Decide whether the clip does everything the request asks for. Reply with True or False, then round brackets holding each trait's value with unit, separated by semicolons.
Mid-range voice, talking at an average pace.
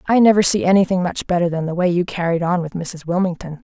False (180 Hz; 245 wpm)